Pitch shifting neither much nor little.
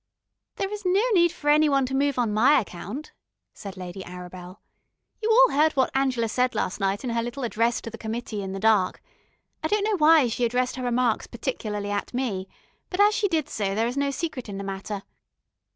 No: wide, 6.3 semitones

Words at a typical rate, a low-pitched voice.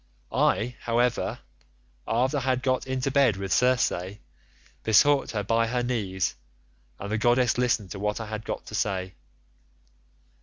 Yes: average, 150 wpm; low, 115 Hz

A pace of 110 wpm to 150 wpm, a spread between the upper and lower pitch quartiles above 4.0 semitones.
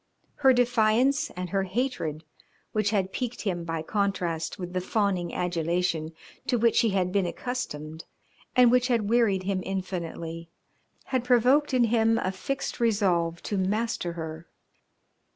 Yes: average, 145 wpm; average, 5.2 semitones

